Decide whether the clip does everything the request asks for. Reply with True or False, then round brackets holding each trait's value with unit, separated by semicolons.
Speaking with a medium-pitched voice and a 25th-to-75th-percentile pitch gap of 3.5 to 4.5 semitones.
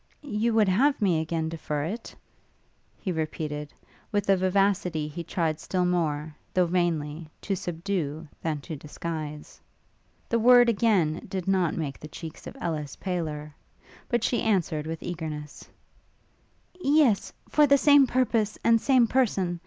False (175 Hz; 5.6 semitones)